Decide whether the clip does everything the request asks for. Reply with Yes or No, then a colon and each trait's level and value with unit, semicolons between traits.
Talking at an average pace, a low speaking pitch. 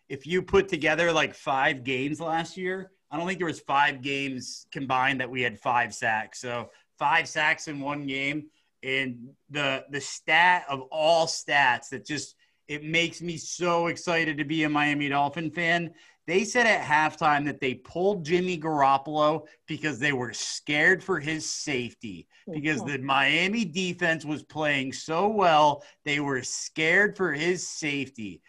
No: average, 165 wpm; medium, 150 Hz